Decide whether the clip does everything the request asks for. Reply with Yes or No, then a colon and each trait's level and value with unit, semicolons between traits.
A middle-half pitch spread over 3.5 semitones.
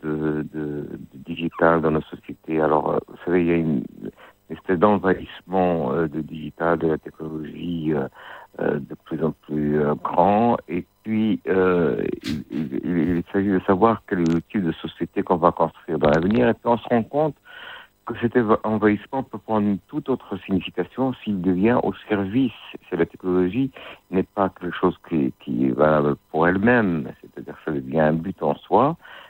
Yes: average, 4.8 semitones